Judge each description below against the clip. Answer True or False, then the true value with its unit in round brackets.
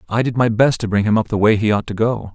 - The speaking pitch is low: True (110 Hz)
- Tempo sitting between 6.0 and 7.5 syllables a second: True (6.5 syllables/s)